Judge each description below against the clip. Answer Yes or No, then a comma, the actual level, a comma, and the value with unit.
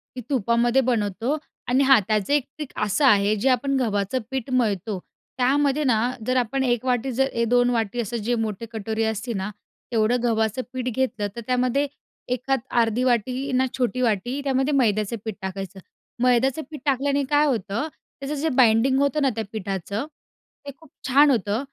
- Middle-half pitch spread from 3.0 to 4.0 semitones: Yes, average, 3.5 semitones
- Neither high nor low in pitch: No, high, 245 Hz